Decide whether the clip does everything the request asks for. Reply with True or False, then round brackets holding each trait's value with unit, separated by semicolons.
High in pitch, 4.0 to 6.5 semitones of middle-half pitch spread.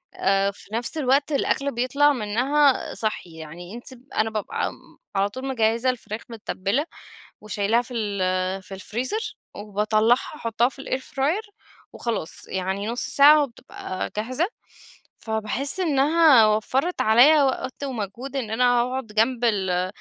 True (235 Hz; 4.6 semitones)